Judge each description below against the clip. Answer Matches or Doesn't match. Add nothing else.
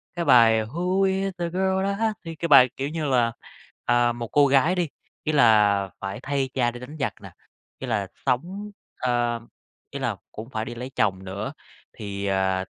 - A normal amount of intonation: Doesn't match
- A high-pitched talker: Doesn't match